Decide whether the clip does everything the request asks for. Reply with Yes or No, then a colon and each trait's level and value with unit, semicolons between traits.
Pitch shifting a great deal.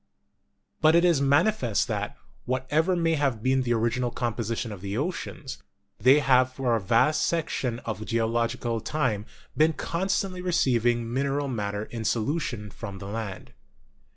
No: average, 4.9 semitones